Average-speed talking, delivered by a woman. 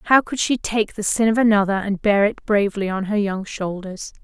No: fast, 225 wpm; female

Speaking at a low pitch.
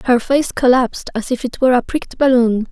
No: very high, 250 Hz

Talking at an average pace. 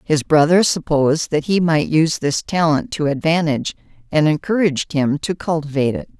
Yes: average, 165 wpm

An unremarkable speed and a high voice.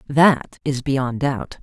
No: average, 150 wpm; low, 135 Hz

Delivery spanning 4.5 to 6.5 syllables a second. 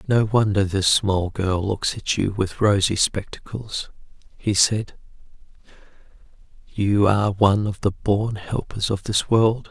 No: 4.1 syllables/s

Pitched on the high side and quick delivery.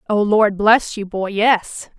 No: high, 210 Hz; average, 180 wpm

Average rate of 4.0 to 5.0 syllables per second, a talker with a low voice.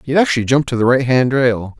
No: 6.6 syllables/s; low, 130 Hz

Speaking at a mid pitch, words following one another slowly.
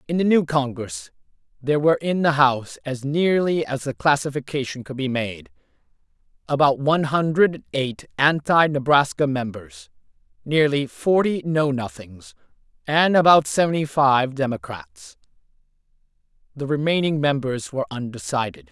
Yes: medium, 145 Hz; slow, 120 wpm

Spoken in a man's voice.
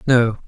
Yes: male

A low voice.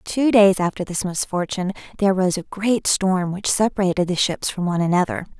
No: high, 190 Hz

